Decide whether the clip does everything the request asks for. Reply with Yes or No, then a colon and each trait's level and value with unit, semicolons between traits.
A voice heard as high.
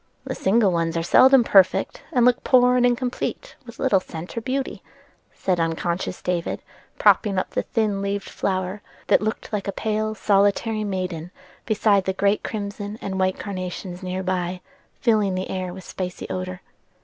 Yes: high, 195 Hz